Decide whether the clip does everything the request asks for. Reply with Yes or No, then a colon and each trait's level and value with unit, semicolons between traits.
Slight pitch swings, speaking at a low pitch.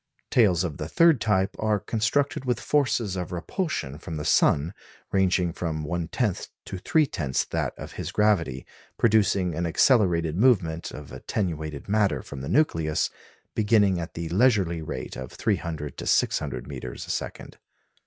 No: average, 5.2 semitones; very low, 90 Hz